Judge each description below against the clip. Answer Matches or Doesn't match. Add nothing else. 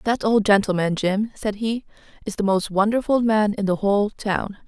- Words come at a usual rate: Matches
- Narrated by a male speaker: Doesn't match